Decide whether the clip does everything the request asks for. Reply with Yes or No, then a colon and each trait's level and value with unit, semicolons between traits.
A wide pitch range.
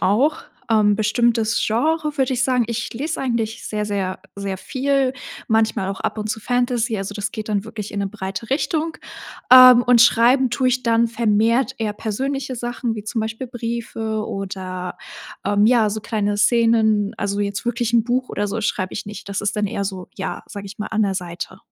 No: average, 3.0 semitones